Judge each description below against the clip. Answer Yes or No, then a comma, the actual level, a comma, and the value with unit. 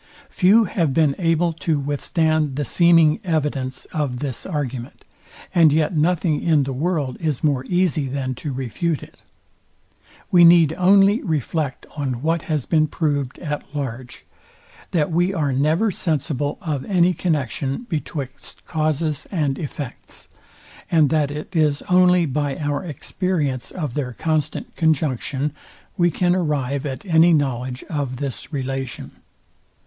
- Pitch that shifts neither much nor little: Yes, average, 3.4 semitones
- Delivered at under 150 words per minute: Yes, average, 140 wpm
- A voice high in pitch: No, medium, 150 Hz